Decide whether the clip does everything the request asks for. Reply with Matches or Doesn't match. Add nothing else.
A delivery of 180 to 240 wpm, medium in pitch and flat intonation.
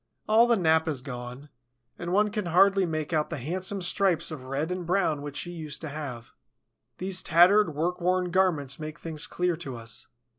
Doesn't match